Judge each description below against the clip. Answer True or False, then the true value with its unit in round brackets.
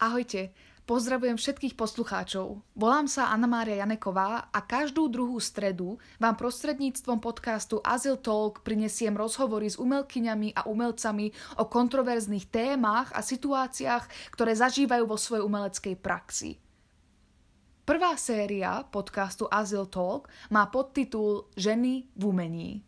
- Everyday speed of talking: True (120 wpm)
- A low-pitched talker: False (220 Hz)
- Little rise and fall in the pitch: False (3.4 semitones)